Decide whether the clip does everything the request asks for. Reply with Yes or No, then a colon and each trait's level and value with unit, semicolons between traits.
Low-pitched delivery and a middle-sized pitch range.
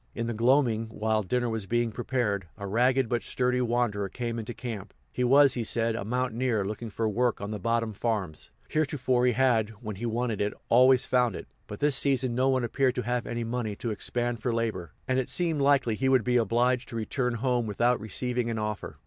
No: low, 120 Hz; narrow, 2.3 semitones